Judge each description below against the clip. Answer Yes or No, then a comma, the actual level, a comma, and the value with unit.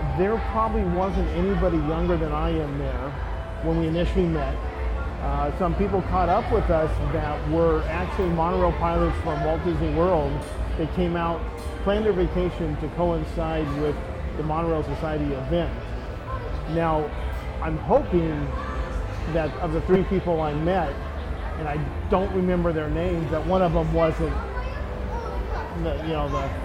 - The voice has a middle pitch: Yes, medium, 155 Hz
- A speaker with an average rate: Yes, average, 150 wpm